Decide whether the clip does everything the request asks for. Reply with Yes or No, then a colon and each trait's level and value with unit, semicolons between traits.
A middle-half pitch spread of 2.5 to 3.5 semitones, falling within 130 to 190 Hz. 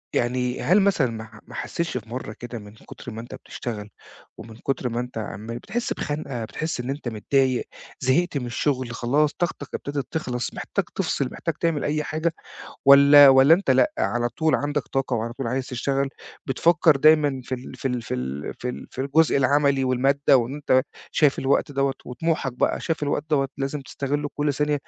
Yes: average, 3.2 semitones; low, 135 Hz